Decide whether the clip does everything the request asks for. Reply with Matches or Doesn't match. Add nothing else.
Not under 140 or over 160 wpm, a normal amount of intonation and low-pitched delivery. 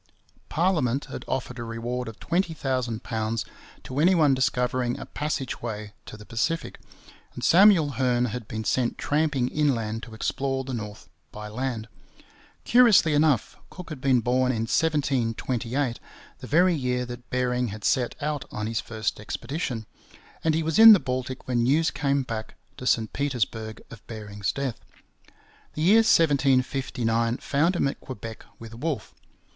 Matches